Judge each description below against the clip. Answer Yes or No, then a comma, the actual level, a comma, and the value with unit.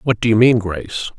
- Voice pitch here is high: No, low, 110 Hz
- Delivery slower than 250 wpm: No, fast, 255 wpm